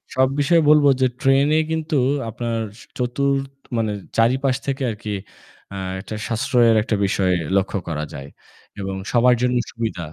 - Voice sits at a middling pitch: No, low, 125 Hz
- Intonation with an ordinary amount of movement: Yes, average, 4.0 semitones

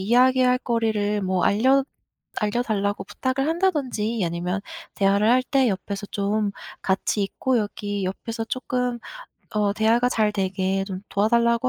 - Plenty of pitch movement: No, average, 3.8 semitones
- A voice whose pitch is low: No, high, 215 Hz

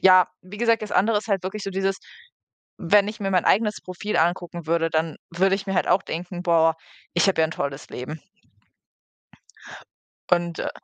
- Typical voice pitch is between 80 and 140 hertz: No, medium, 185 Hz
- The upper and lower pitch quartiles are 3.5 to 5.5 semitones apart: No, average, 2.9 semitones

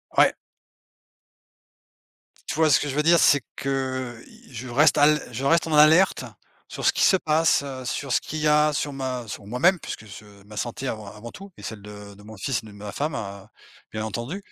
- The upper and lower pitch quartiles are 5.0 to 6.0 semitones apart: Yes, wide, 5.6 semitones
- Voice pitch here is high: No, low, 130 Hz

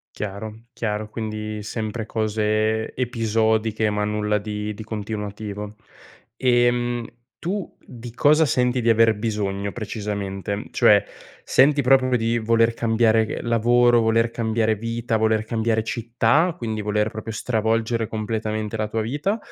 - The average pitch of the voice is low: Yes, low, 110 Hz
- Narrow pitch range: Yes, narrow, 1.7 semitones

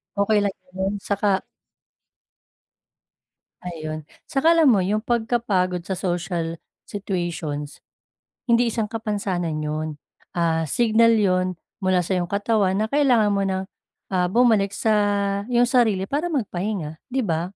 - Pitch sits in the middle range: No, high, 200 Hz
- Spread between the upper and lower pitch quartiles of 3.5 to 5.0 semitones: Yes, average, 4.1 semitones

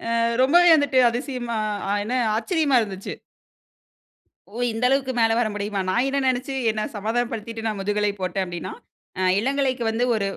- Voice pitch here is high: Yes, high, 235 Hz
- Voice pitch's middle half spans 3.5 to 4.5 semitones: Yes, average, 4.0 semitones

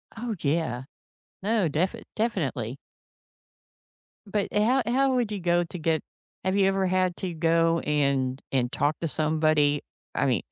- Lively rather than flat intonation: No, average, 5.0 semitones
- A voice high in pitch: No, medium, 165 Hz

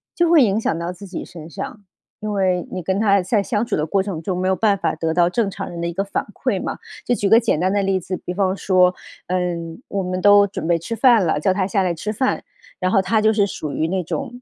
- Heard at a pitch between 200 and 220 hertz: No, high, 190 Hz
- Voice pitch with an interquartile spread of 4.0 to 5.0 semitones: No, narrow, 2.6 semitones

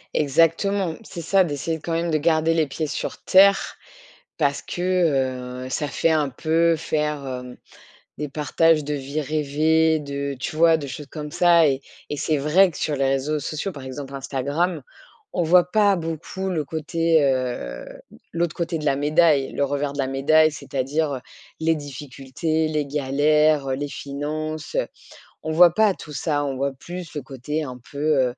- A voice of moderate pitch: Yes, medium, 150 Hz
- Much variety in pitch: No, average, 2.8 semitones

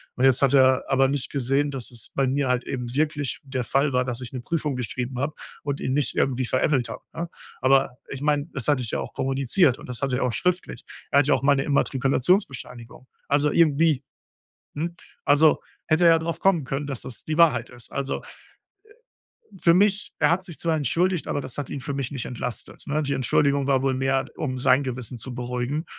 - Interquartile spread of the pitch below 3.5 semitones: Yes, average, 2.7 semitones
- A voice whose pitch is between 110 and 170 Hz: Yes, low, 135 Hz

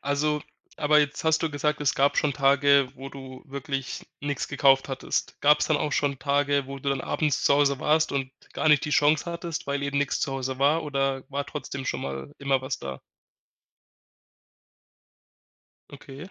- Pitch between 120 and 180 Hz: Yes, medium, 140 Hz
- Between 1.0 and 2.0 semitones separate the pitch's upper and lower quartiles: Yes, narrow, 1.5 semitones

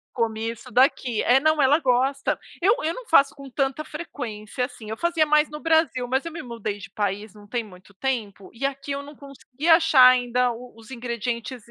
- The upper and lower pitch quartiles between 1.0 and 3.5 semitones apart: No, average, 4.0 semitones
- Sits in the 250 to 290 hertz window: Yes, very high, 255 Hz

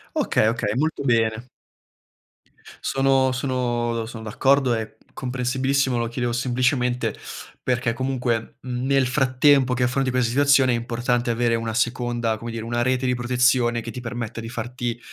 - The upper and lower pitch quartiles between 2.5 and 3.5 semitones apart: No, narrow, 1.7 semitones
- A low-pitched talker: Yes, low, 125 Hz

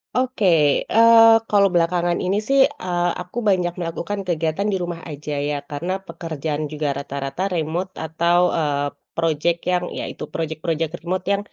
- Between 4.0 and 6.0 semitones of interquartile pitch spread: No, average, 2.9 semitones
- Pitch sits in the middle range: Yes, medium, 170 Hz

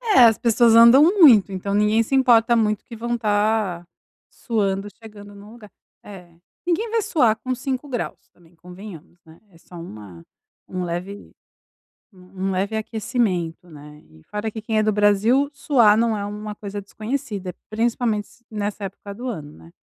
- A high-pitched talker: Yes, high, 210 Hz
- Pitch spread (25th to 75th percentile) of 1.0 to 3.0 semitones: No, average, 3.6 semitones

